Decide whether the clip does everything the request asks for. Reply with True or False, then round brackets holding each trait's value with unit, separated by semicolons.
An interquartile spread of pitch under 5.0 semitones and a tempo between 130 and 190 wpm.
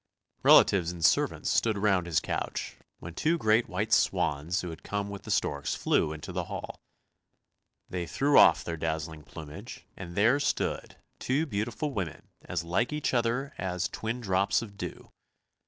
False (5.4 semitones; 165 wpm)